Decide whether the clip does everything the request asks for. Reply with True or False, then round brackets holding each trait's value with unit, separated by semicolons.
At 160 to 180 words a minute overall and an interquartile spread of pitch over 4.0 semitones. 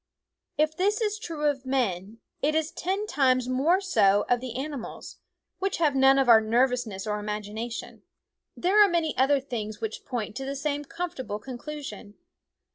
True (165 wpm; 5.5 semitones)